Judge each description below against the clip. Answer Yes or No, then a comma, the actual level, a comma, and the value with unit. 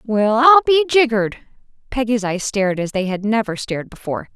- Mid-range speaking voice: No, high, 230 Hz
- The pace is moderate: Yes, average, 180 wpm